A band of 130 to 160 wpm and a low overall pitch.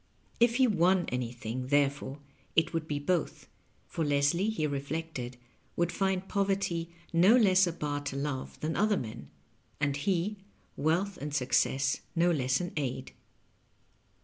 No: average, 145 wpm; medium, 160 Hz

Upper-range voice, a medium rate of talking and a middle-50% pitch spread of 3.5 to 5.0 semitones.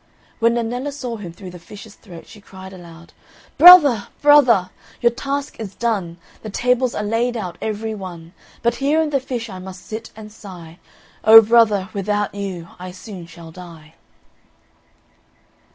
Yes: high, 210 Hz; average, 160 wpm; average, 4.5 semitones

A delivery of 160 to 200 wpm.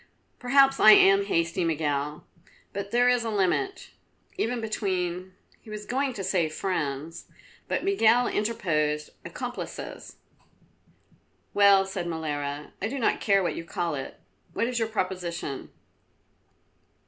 No: slow, 135 wpm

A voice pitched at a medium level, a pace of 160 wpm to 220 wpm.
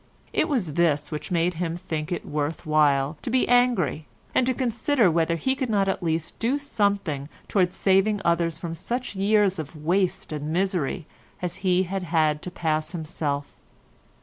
Yes: medium, 175 Hz; average, 175 wpm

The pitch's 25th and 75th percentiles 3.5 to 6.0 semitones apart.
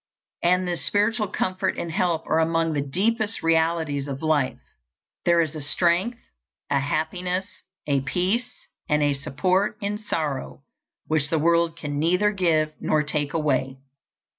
Yes: average, 3.8 semitones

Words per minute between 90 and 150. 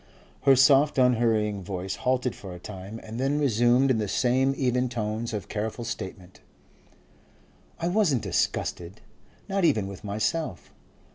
Yes: average, 140 wpm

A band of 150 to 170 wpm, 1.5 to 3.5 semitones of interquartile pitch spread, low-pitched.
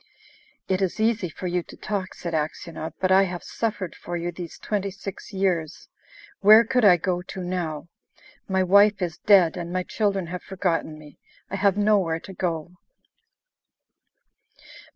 No: average, 160 wpm; narrow, 2.5 semitones; medium, 185 Hz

